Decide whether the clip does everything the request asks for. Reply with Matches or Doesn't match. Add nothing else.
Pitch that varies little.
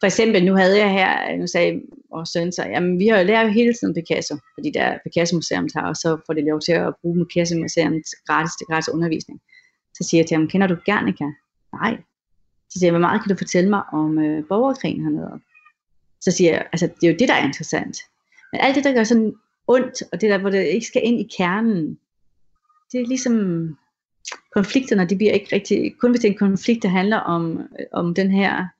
Doesn't match